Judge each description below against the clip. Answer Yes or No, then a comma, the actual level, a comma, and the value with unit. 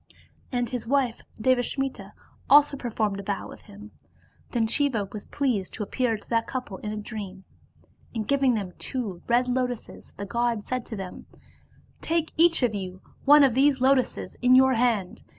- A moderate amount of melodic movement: Yes, average, 3.8 semitones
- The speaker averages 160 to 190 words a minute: Yes, average, 170 wpm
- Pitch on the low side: No, high, 240 Hz